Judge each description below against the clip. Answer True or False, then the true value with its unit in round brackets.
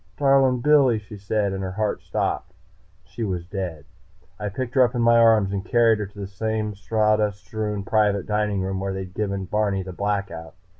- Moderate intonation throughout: False (2.3 semitones)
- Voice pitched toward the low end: True (105 Hz)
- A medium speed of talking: True (195 wpm)